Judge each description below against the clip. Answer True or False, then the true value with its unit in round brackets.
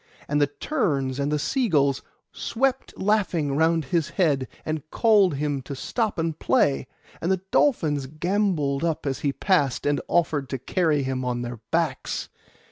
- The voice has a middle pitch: True (150 Hz)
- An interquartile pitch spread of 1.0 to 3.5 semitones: False (4.7 semitones)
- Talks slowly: False (170 wpm)